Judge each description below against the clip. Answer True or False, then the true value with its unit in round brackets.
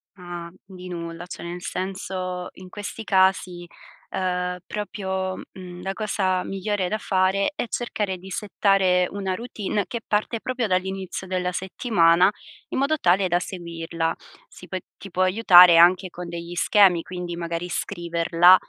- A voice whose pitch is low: False (185 Hz)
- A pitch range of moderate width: False (1.8 semitones)